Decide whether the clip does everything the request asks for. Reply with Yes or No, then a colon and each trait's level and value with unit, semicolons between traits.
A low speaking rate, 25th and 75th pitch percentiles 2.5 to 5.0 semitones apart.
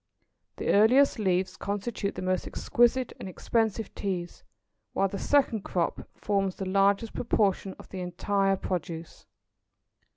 Yes: slow, 130 wpm; average, 2.8 semitones